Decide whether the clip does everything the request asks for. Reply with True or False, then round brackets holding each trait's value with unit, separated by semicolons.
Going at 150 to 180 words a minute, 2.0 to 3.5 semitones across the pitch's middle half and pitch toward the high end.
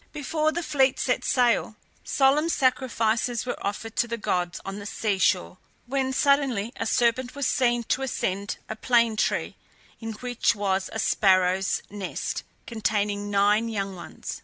False (155 wpm; 4.1 semitones; 225 Hz)